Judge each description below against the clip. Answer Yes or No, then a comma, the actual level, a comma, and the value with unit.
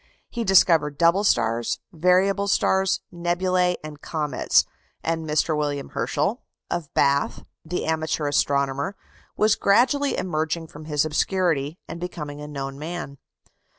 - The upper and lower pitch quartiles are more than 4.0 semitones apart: No, average, 3.7 semitones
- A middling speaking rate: No, slow, 125 wpm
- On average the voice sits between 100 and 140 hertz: No, medium, 160 Hz